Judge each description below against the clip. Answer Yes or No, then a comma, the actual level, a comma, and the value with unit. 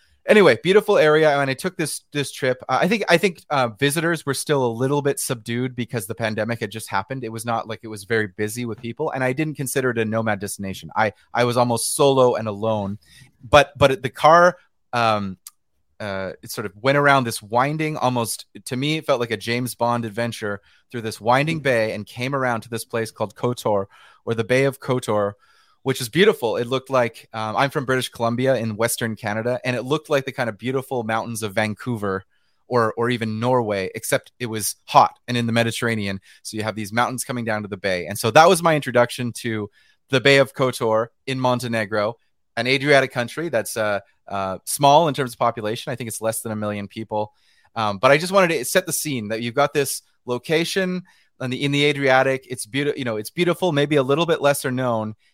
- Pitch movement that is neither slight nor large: Yes, average, 3.9 semitones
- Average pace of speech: No, fast, 220 wpm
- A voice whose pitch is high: No, low, 120 Hz